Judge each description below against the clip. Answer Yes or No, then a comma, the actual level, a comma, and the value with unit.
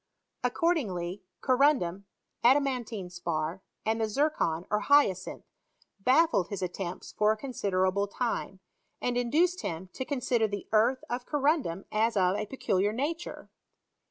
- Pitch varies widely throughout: Yes, wide, 5.8 semitones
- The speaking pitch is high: Yes, high, 220 Hz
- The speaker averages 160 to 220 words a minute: No, average, 140 wpm